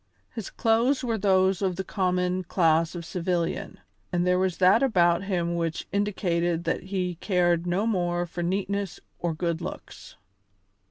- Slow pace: No, average, 155 wpm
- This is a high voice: No, medium, 180 Hz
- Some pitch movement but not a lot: No, narrow, 2.1 semitones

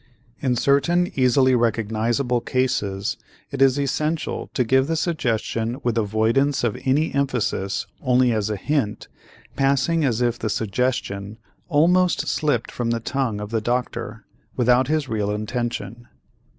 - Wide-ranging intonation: No, average, 3.7 semitones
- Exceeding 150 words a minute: No, slow, 135 wpm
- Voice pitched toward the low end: Yes, low, 125 Hz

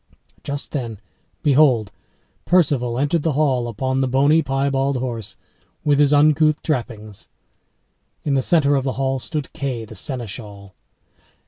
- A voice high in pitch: No, low, 135 Hz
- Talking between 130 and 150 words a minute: Yes, slow, 135 wpm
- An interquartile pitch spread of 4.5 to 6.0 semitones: No, average, 3.4 semitones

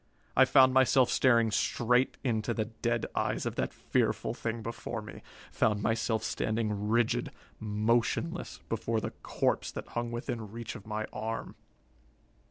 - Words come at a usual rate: Yes, average, 145 wpm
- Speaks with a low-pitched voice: Yes, low, 115 Hz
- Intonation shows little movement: Yes, narrow, 1.6 semitones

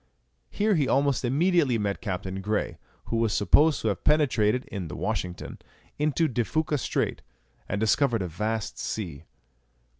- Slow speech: No, average, 150 wpm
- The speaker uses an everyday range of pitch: No, wide, 6.3 semitones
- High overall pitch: No, low, 115 Hz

